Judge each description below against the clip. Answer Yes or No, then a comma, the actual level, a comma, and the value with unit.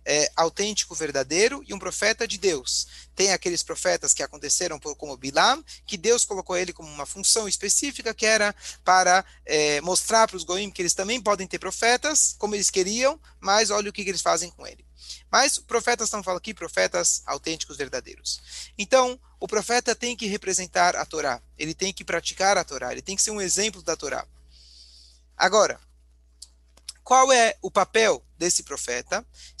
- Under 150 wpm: No, average, 175 wpm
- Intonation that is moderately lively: No, wide, 6.0 semitones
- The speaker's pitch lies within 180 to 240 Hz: Yes, medium, 185 Hz